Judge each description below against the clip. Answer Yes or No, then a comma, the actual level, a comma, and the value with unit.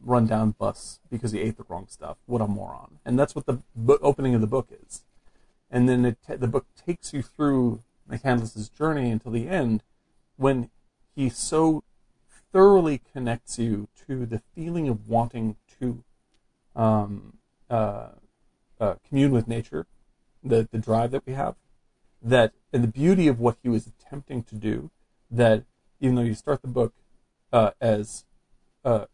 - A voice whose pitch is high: No, low, 120 Hz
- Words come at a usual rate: Yes, average, 170 wpm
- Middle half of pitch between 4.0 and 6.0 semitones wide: No, average, 3.1 semitones